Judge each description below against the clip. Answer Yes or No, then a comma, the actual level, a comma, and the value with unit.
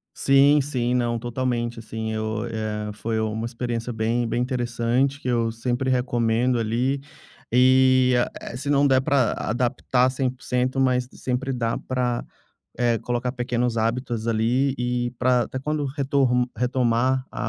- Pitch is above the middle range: No, low, 125 Hz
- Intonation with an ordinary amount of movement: No, narrow, 1.9 semitones